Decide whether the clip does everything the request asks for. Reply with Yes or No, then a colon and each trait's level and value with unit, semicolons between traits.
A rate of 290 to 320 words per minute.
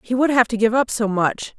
Yes: fast, 305 wpm